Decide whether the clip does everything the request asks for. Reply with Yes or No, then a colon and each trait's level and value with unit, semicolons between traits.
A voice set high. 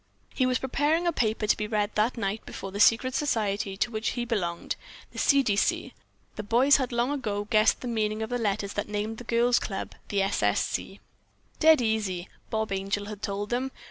Yes: high, 220 Hz